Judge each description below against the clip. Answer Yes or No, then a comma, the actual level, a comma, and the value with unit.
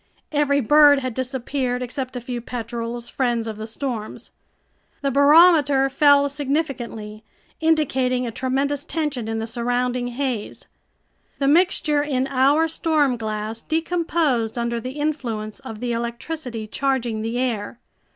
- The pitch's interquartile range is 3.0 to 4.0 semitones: Yes, average, 3.5 semitones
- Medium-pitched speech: No, very high, 255 Hz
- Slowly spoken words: Yes, slow, 130 wpm